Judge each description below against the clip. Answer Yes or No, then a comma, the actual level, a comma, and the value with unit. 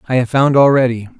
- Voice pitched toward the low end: Yes, low, 125 Hz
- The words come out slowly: No, average, 200 wpm